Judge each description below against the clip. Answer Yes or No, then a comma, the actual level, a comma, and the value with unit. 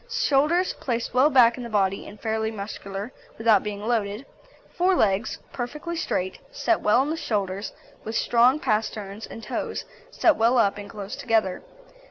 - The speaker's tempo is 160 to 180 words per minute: Yes, average, 165 wpm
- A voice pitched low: No, high, 225 Hz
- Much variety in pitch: No, average, 4.3 semitones